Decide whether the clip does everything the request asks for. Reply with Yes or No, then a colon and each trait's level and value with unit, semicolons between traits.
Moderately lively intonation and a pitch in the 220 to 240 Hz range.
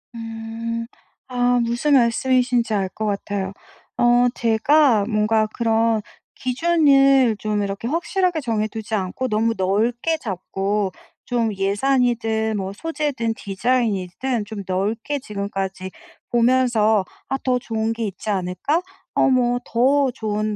Yes: average, 3.3 semitones; high, 230 Hz